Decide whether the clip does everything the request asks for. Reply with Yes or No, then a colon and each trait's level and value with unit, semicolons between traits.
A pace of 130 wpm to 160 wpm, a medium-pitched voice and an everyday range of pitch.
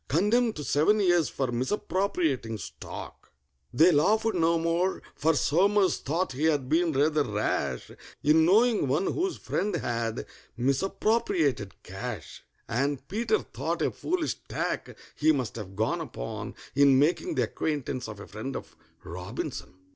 No: average, 140 wpm; medium, 150 Hz; wide, 6.9 semitones